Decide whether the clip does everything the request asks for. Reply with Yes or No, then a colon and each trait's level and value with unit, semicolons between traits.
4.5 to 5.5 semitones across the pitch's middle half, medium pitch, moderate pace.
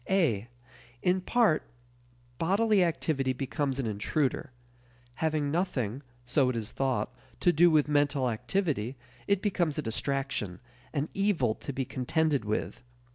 No: average, 5.1 semitones; medium, 145 Hz; slow, 130 wpm